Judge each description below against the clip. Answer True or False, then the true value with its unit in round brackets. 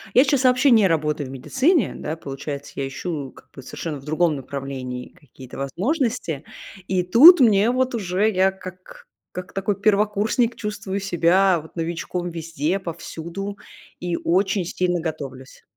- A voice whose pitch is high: False (180 Hz)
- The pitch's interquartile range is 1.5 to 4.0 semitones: False (5.2 semitones)